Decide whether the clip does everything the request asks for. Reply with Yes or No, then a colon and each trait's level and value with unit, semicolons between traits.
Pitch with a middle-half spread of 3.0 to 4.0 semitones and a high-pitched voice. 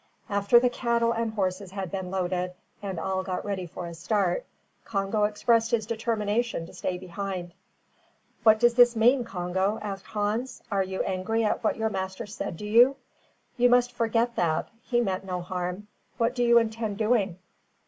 Yes: average, 3.6 semitones; high, 210 Hz